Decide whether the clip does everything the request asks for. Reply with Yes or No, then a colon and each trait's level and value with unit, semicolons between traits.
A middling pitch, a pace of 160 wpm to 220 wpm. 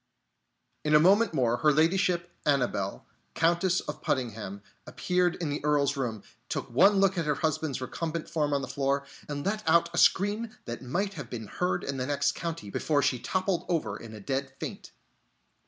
Yes: medium, 150 Hz; average, 185 wpm